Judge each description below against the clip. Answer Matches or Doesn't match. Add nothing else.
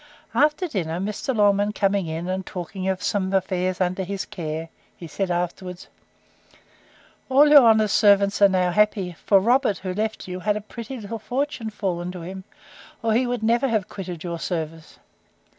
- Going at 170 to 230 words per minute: Matches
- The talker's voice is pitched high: Matches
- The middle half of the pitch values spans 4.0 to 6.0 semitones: Doesn't match